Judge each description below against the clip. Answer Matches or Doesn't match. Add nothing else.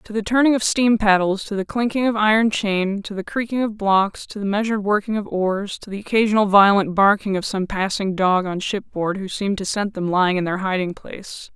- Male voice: Doesn't match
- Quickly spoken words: Matches